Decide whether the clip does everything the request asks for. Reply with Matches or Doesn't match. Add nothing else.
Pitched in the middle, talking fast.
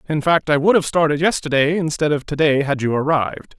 Matches